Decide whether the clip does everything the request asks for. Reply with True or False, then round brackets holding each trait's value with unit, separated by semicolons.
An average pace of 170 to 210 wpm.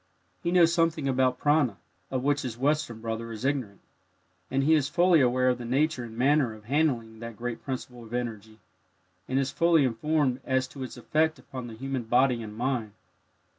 True (190 wpm)